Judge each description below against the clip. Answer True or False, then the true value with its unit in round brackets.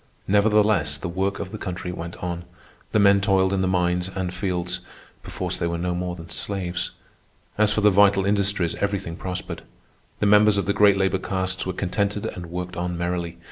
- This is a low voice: True (95 Hz)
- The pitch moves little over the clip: True (2.2 semitones)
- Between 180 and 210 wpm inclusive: True (185 wpm)